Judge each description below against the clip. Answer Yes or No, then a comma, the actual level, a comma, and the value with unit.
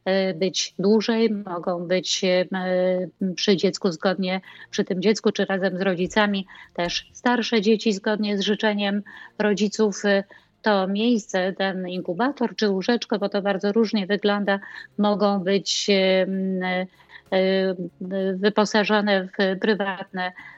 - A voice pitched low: No, high, 195 Hz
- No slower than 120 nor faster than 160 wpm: No, slow, 110 wpm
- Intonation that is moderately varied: No, narrow, 2.0 semitones